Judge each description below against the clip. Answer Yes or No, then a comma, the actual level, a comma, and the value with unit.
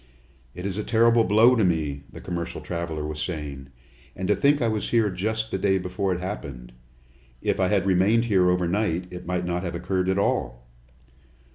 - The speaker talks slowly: No, average, 195 wpm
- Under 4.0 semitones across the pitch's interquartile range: Yes, average, 3.5 semitones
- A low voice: Yes, very low, 90 Hz